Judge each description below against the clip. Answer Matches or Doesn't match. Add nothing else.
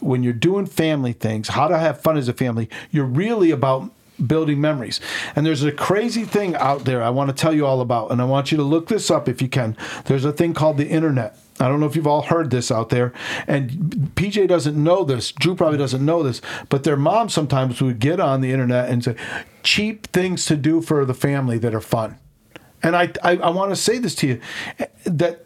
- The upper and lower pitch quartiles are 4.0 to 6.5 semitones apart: Matches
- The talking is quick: Matches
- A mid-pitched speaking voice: Matches